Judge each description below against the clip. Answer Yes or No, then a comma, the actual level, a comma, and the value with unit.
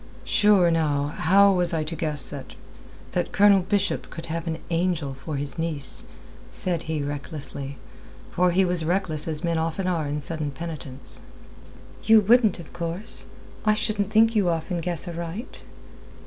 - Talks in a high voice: No, medium, 170 Hz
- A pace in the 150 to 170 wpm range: Yes, average, 160 wpm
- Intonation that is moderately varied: Yes, average, 3.5 semitones